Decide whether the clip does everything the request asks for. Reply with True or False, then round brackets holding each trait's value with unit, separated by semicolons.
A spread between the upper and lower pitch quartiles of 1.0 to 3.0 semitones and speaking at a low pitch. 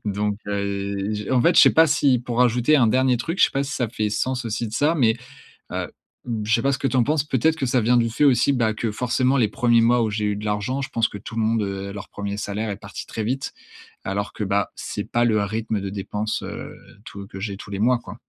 False (3.6 semitones; 115 Hz)